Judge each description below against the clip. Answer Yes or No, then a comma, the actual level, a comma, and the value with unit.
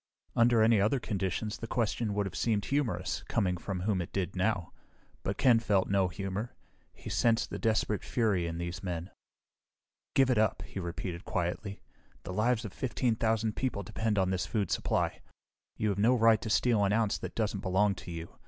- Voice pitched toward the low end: Yes, low, 105 Hz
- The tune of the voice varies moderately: Yes, average, 3.3 semitones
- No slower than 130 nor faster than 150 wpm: No, average, 190 wpm